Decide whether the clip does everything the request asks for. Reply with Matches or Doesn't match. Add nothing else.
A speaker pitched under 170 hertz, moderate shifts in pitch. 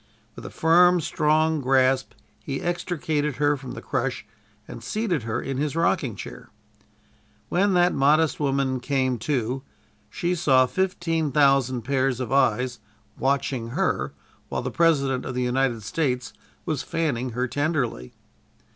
Matches